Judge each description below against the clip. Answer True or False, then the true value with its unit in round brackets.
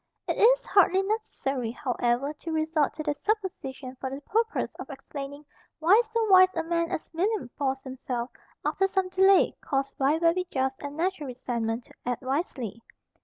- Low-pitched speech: False (300 Hz)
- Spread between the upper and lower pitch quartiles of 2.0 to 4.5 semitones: False (6.1 semitones)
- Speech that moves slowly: False (170 wpm)